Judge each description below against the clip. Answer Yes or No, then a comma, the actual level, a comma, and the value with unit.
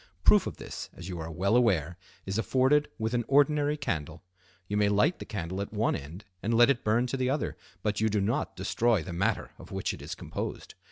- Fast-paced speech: Yes, fast, 225 wpm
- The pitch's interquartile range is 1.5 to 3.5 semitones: No, average, 5.0 semitones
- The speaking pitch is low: Yes, low, 105 Hz